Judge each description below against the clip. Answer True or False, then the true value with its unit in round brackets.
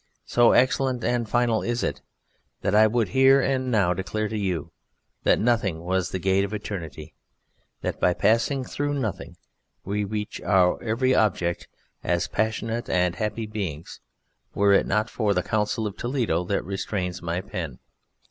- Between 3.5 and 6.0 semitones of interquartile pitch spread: True (4.3 semitones)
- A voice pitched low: True (105 Hz)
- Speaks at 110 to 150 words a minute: False (160 wpm)